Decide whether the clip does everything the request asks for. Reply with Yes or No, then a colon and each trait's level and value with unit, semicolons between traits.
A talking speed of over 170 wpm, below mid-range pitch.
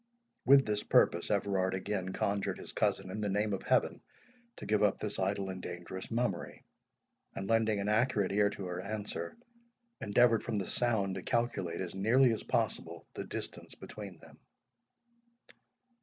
No: average, 160 wpm; low, 100 Hz